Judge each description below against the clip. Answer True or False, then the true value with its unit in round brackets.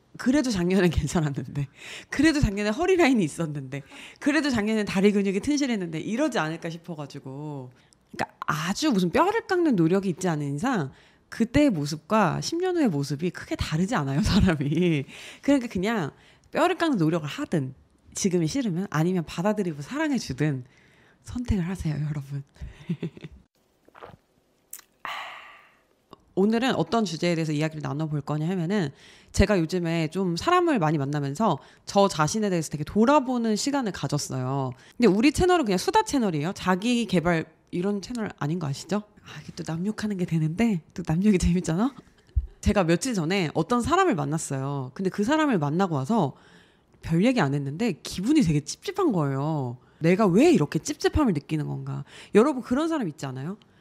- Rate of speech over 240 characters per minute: True (355 characters per minute)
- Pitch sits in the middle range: True (180 Hz)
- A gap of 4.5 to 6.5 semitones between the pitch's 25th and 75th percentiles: False (7.5 semitones)